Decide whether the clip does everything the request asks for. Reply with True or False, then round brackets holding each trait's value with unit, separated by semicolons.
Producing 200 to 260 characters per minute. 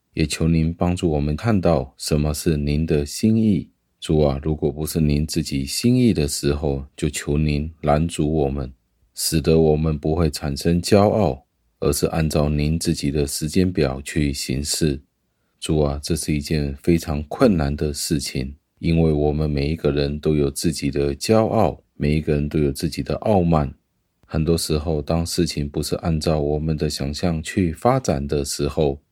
True (250 characters per minute)